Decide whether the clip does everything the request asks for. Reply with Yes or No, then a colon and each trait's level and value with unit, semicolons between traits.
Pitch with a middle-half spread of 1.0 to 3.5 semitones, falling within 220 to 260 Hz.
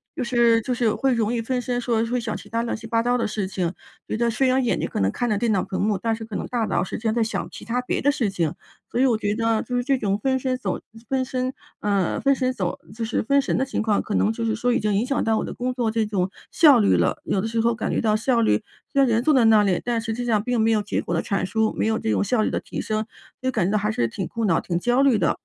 Yes: narrow, 2.6 semitones; high, 225 Hz